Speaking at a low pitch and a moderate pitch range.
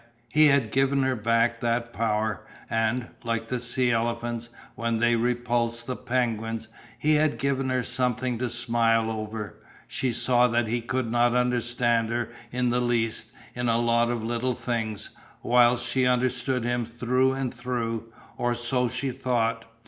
No: low, 120 Hz; narrow, 1.4 semitones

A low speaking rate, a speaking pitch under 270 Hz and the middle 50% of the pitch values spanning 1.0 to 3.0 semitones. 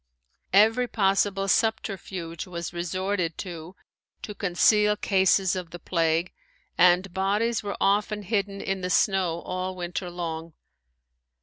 Yes: slow, 120 wpm; high, 190 Hz; narrow, 2.5 semitones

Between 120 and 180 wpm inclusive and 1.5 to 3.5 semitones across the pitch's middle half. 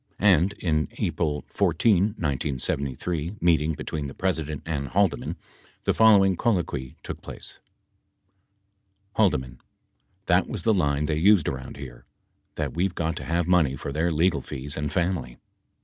No: average, 150 wpm; average, 4.1 semitones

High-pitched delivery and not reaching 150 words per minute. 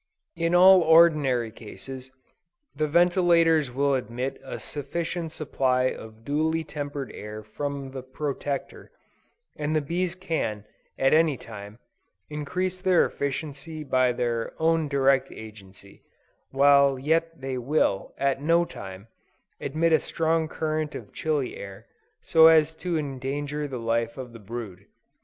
No: medium, 140 Hz; slow, 135 wpm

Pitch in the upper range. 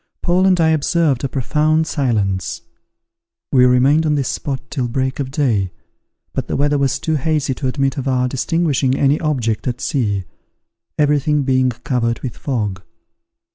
No: low, 135 Hz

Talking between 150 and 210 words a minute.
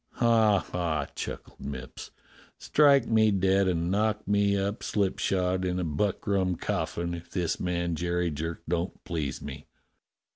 No: average, 140 wpm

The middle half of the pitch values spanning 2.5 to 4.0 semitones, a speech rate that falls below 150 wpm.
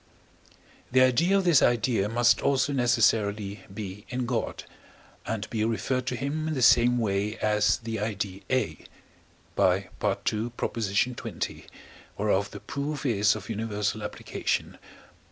Yes: average, 3.6 semitones; slow, 135 wpm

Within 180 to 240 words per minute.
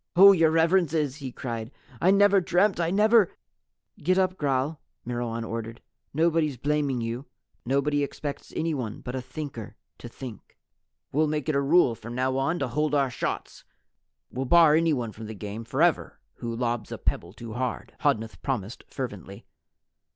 No: average, 165 wpm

